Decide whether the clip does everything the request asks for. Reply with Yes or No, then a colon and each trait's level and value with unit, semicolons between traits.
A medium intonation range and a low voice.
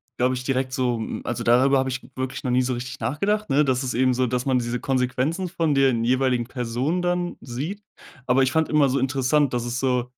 No: narrow, 2.1 semitones; low, 130 Hz